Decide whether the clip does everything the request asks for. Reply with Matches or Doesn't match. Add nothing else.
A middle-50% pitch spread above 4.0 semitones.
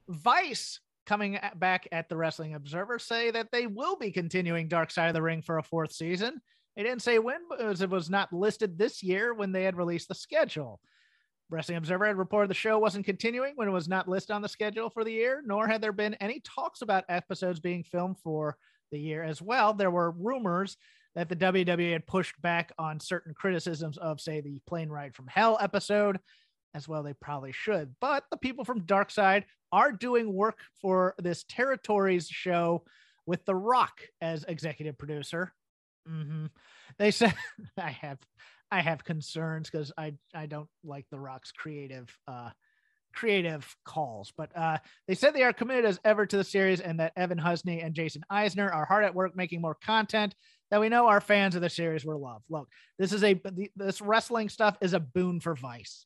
Matches